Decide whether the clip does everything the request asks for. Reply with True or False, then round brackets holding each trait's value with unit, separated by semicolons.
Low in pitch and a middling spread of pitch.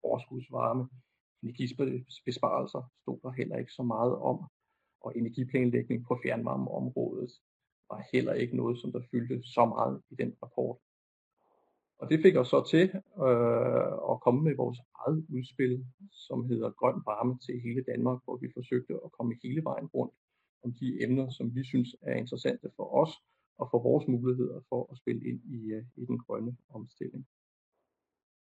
False (125 Hz; 1.3 semitones)